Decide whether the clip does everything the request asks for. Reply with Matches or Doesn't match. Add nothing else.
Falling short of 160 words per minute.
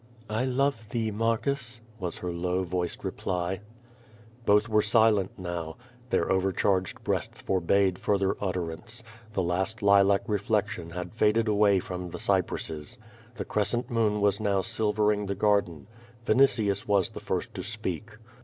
Matches